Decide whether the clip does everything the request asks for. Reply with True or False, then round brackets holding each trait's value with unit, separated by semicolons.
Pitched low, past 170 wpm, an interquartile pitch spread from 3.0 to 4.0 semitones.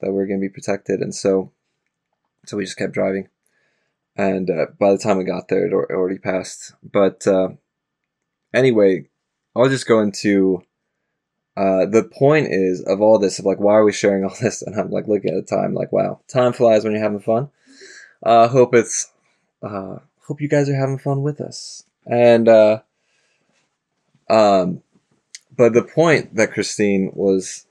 True (105 Hz; 185 wpm; 3.6 semitones)